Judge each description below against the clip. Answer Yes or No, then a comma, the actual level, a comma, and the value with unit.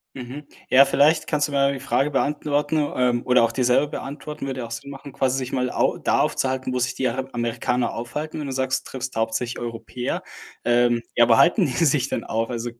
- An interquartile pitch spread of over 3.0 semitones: No, narrow, 2.5 semitones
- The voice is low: Yes, low, 130 Hz